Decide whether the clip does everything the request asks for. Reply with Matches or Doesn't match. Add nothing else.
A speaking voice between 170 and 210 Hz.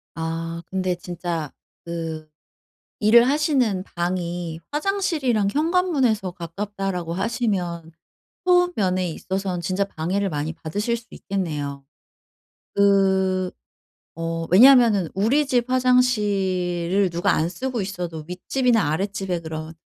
Matches